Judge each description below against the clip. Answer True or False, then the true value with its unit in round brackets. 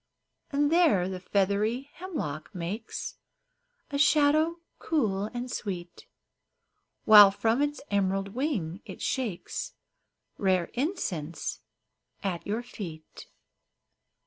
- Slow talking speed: True (95 wpm)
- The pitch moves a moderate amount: False (7.1 semitones)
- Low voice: False (210 Hz)